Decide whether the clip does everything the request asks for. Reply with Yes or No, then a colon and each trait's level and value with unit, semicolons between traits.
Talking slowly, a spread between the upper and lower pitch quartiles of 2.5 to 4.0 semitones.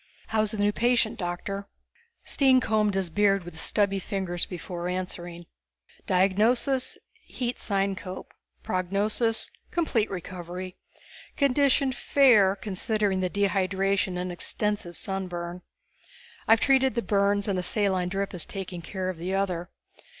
Yes: slow, 125 wpm; average, 2.8 semitones